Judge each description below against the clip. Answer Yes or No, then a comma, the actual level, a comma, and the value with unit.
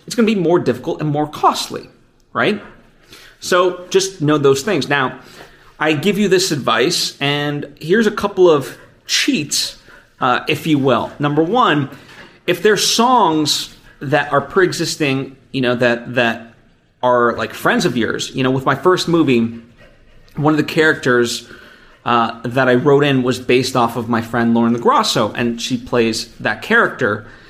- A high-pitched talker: No, medium, 140 Hz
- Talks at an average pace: Yes, average, 165 wpm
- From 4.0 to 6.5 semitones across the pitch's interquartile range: Yes, average, 5.1 semitones